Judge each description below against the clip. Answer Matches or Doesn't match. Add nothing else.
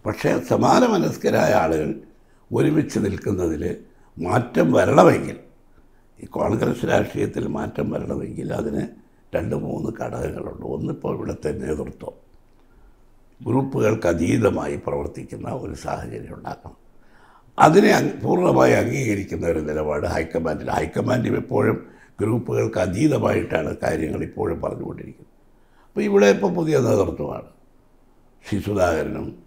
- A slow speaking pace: Doesn't match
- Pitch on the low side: Matches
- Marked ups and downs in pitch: Matches